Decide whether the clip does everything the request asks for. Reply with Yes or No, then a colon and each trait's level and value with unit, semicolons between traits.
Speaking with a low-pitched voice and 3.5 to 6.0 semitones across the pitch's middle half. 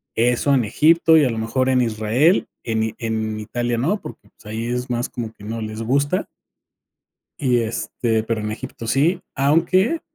Yes: low, 120 Hz; average, 4.1 semitones